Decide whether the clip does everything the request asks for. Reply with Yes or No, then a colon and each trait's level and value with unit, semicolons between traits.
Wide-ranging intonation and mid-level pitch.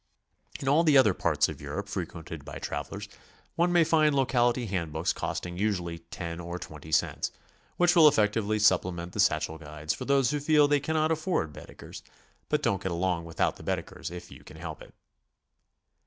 No: wide, 8.9 semitones; very low, 95 Hz